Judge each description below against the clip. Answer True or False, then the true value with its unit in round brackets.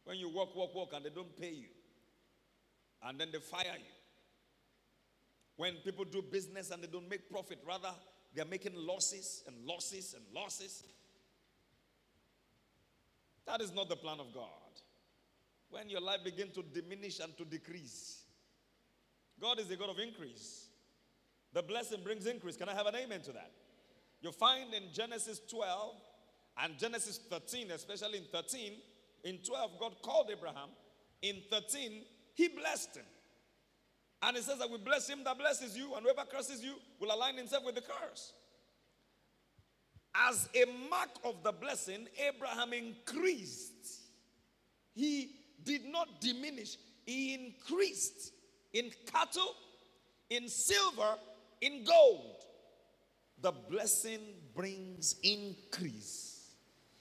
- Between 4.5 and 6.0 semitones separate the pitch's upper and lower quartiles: True (5.6 semitones)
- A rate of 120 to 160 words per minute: True (140 wpm)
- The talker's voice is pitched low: False (215 Hz)